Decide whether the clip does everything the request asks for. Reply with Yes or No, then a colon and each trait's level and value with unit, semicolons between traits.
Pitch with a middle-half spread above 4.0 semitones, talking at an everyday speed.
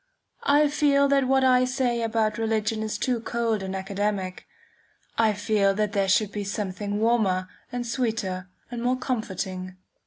No: average, 3.5 semitones; average, 155 wpm